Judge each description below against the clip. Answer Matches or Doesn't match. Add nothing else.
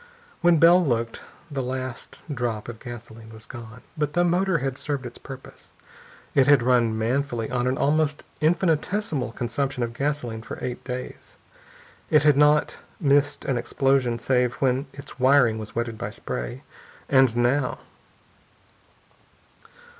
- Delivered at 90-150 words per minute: Matches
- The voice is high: Doesn't match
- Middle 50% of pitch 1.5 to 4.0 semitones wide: Matches